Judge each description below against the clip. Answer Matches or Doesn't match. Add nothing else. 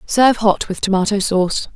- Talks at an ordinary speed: Matches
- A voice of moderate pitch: Doesn't match